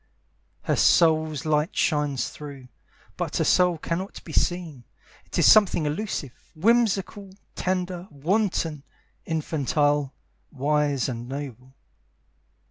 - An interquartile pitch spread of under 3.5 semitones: No, average, 4.1 semitones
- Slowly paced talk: Yes, slow, 105 wpm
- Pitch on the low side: No, medium, 155 Hz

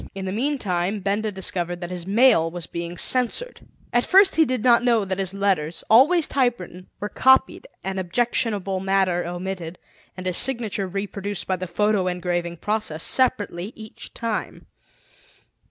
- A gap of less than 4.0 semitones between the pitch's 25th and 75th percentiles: No, average, 4.6 semitones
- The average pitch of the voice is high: Yes, high, 195 Hz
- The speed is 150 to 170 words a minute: Yes, average, 155 wpm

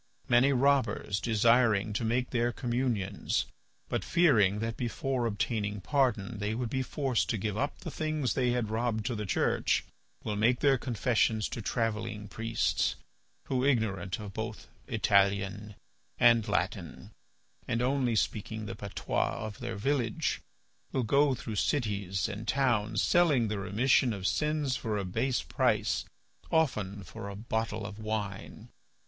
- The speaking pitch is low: Yes, low, 115 Hz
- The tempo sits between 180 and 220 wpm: No, average, 145 wpm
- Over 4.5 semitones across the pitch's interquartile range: No, average, 3.4 semitones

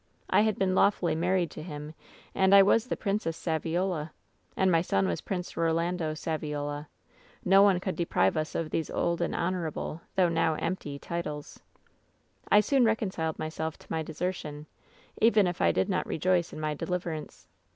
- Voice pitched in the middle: Yes, medium, 170 Hz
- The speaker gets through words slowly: No, average, 170 wpm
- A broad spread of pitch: No, average, 3.2 semitones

